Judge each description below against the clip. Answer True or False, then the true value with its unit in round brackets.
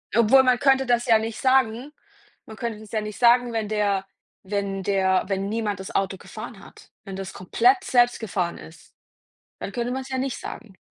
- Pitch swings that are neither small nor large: True (3.9 semitones)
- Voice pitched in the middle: False (220 Hz)